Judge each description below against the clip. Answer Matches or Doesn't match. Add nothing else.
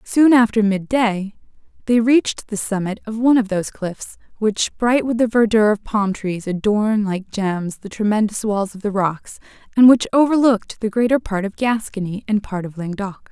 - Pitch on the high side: Matches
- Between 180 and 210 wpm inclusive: Matches